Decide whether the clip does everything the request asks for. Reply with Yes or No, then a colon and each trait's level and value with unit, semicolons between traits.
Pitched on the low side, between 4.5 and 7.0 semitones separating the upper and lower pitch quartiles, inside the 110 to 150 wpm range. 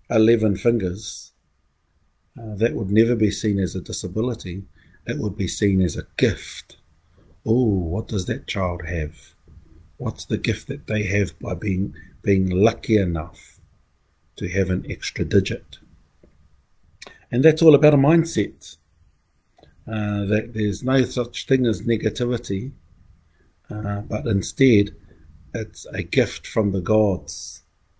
Yes: low, 100 Hz; average, 5.1 semitones; slow, 135 wpm